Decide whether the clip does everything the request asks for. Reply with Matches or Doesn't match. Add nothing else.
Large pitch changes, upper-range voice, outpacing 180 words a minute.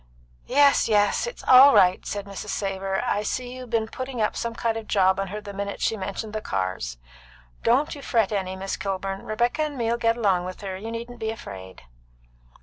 Doesn't match